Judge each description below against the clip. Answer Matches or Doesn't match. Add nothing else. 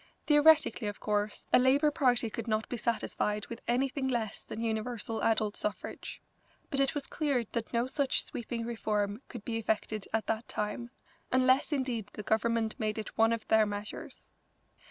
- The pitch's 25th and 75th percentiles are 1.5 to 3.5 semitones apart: Matches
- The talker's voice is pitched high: Matches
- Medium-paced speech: Matches